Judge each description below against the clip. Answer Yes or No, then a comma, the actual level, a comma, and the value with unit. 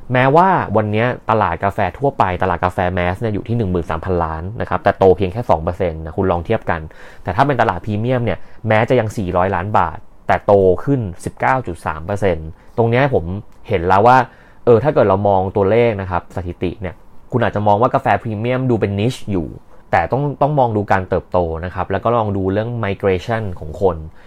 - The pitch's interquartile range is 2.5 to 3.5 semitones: No, average, 4.3 semitones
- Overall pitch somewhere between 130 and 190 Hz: No, low, 100 Hz